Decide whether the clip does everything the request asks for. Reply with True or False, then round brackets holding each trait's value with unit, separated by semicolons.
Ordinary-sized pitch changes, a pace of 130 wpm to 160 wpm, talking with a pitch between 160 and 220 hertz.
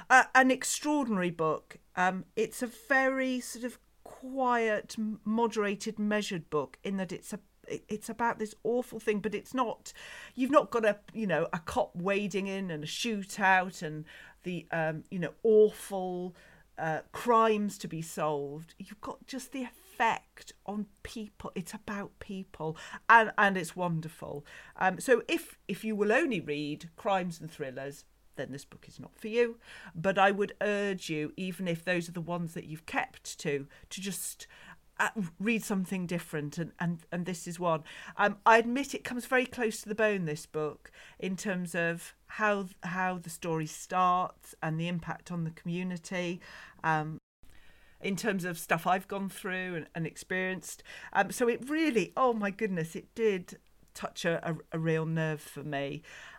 False (4.5 semitones; 170 wpm; 190 Hz)